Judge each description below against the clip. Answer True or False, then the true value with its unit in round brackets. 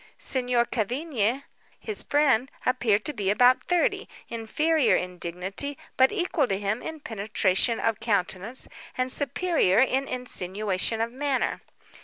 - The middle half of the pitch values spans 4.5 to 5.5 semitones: True (5.0 semitones)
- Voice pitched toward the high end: True (240 Hz)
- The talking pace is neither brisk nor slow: False (125 wpm)